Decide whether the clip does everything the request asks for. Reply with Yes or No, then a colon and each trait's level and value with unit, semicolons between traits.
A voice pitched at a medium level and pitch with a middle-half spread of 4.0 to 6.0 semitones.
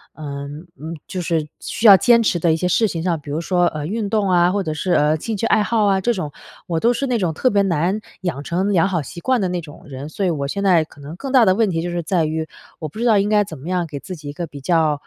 Yes: medium, 175 Hz; average, 4.4 semitones